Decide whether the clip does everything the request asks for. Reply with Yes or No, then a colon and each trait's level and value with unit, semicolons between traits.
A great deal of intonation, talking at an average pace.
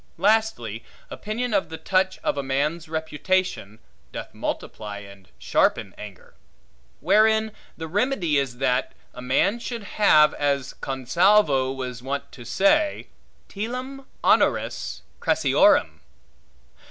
No: wide, 8.3 semitones; slow, 115 wpm